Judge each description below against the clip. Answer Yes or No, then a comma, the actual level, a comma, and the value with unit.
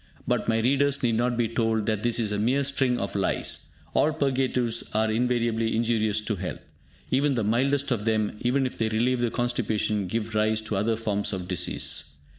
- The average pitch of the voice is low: Yes, low, 115 Hz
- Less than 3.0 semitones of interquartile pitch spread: Yes, narrow, 2.4 semitones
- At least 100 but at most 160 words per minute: No, average, 195 wpm